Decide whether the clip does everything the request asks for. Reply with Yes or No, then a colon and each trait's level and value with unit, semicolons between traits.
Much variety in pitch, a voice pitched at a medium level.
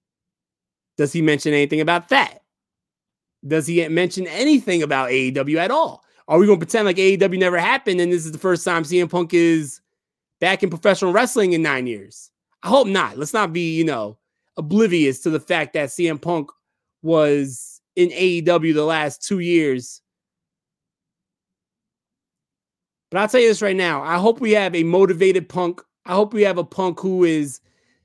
No: average, 3.3 semitones; medium, 175 Hz